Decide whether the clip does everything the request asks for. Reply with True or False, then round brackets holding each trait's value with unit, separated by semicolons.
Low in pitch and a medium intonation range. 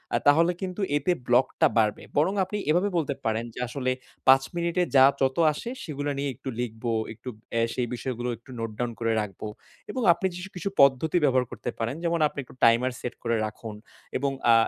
False (130 Hz; 5.7 semitones)